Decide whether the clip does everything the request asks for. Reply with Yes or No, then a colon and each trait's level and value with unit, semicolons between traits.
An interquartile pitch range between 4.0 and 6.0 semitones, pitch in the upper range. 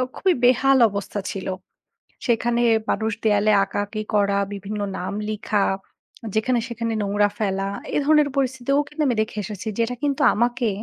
No: average, 3.5 semitones; high, 220 Hz